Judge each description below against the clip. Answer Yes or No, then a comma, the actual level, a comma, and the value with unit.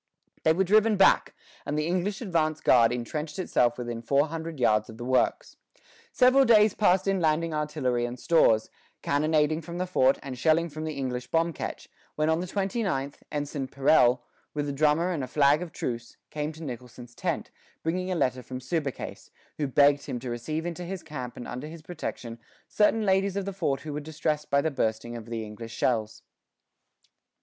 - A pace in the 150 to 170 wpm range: No, average, 195 wpm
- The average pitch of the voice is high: No, medium, 150 Hz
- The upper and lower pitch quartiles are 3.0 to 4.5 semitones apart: No, average, 5.1 semitones